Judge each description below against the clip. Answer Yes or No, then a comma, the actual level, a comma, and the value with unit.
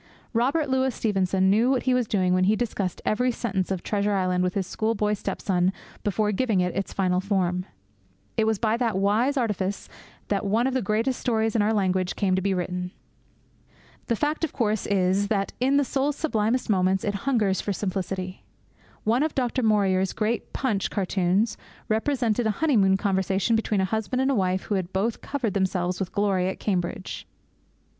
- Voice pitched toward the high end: Yes, high, 205 Hz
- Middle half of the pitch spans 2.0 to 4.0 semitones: Yes, average, 3.5 semitones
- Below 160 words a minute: No, average, 185 wpm